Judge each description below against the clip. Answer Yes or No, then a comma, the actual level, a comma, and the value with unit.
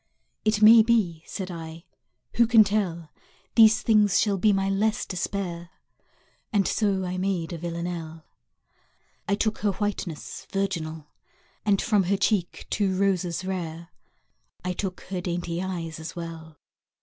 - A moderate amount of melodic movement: Yes, average, 3.4 semitones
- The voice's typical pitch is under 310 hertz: Yes, medium, 185 Hz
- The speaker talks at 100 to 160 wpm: Yes, average, 140 wpm